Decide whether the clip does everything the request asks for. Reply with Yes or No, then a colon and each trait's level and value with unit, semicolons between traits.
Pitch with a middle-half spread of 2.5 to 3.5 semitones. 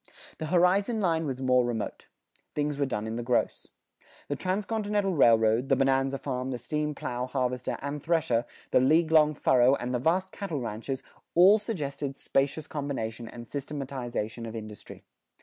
No: average, 4.6 semitones